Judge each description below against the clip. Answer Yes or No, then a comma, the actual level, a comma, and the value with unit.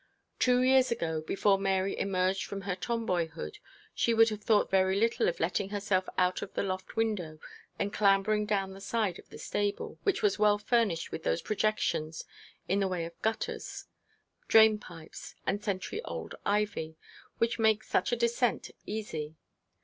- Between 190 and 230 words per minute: No, average, 165 wpm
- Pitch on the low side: No, high, 200 Hz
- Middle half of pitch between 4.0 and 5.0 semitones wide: No, average, 2.9 semitones